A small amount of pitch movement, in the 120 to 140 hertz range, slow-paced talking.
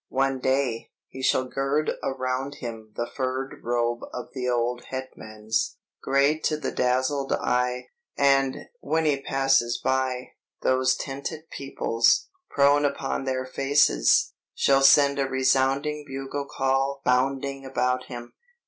Yes: narrow, 1.5 semitones; low, 135 Hz; slow, 130 wpm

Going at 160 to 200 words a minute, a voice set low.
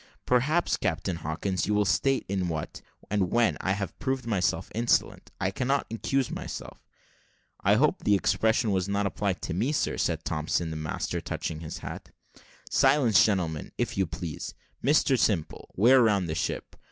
Yes: average, 165 wpm; low, 100 Hz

